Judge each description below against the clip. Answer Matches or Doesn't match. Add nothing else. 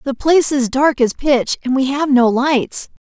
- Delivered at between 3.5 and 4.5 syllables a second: Matches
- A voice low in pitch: Doesn't match